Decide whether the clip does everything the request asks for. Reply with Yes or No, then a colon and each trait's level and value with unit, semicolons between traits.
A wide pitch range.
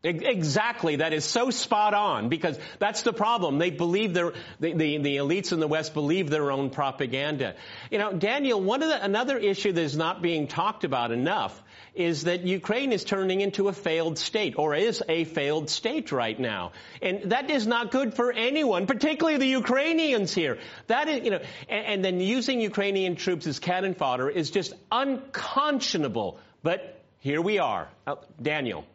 Yes: wide, 6.5 semitones